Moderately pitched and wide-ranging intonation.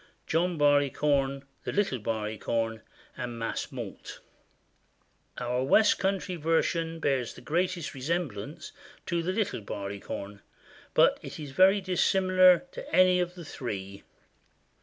Yes: medium, 150 Hz; wide, 7.4 semitones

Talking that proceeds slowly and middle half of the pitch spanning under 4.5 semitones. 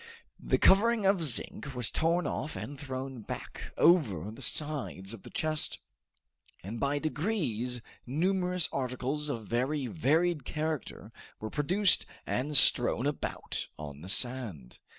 No: slow, 130 wpm; average, 5.0 semitones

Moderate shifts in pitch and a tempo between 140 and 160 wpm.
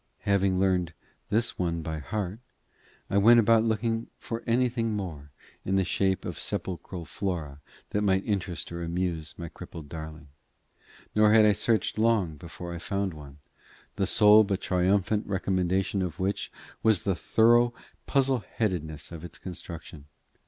Yes: average, 4.1 semitones; average, 150 wpm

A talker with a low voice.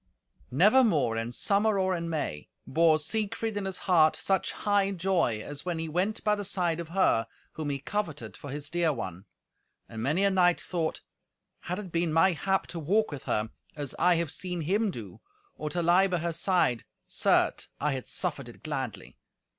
No: medium, 170 Hz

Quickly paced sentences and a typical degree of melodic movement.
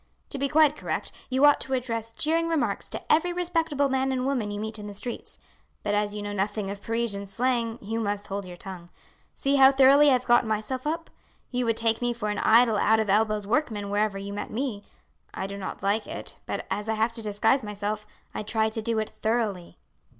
Yes: fast, 225 wpm; average, 4.1 semitones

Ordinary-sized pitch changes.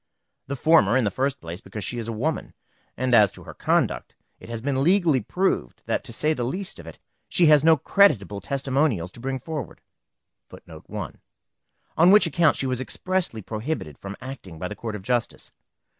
No: wide, 6.7 semitones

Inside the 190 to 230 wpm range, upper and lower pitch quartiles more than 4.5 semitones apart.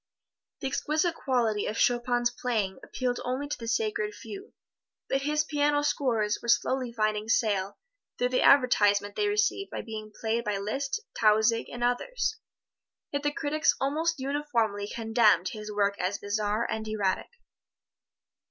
No: average, 145 wpm; average, 5.3 semitones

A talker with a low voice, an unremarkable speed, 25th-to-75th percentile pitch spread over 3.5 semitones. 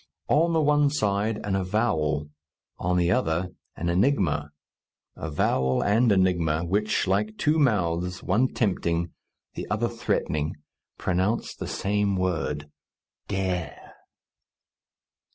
No: very low, 95 Hz; slow, 110 wpm; average, 4.2 semitones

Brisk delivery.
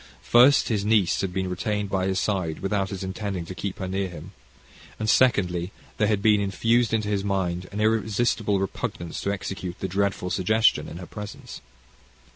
No: average, 180 wpm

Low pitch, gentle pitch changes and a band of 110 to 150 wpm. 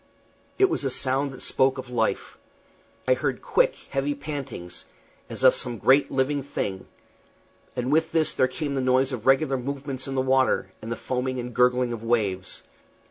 No: low, 130 Hz; narrow, 2.1 semitones; average, 180 wpm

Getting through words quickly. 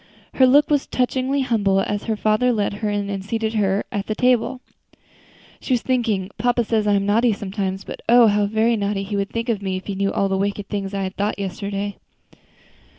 Yes: fast, 210 wpm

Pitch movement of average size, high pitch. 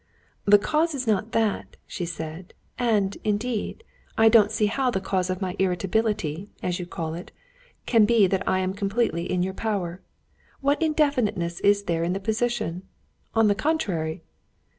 Yes: average, 3.8 semitones; high, 200 Hz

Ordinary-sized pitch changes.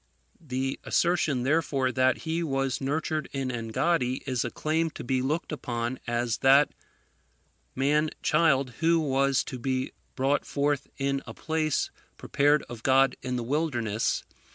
Yes: average, 3.1 semitones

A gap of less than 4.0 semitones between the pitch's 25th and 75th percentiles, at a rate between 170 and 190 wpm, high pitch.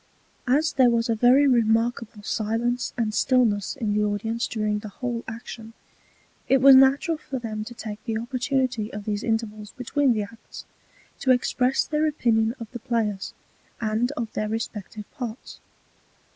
No: average, 2.7 semitones; average, 160 wpm; high, 230 Hz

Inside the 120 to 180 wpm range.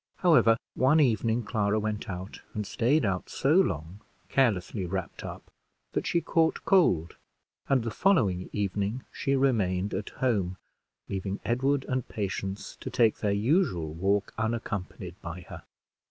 Yes: average, 140 wpm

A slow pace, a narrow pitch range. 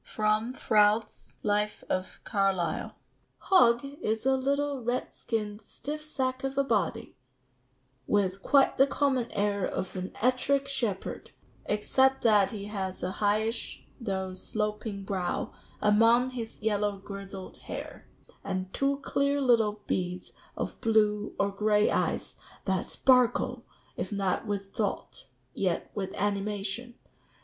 No: slow, 125 wpm; average, 4.0 semitones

